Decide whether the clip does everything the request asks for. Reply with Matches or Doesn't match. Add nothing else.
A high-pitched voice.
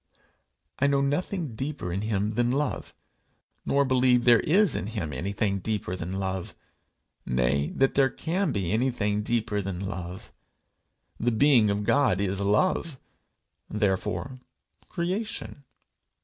Doesn't match